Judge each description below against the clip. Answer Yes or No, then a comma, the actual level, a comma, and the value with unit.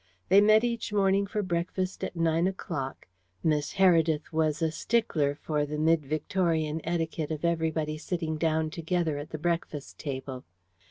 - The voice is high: No, medium, 160 Hz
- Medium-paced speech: Yes, average, 155 wpm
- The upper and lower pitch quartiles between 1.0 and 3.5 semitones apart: Yes, average, 2.7 semitones